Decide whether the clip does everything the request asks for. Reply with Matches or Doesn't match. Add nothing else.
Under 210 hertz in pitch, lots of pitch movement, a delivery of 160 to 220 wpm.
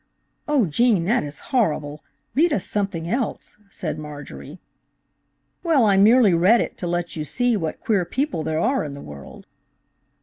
Matches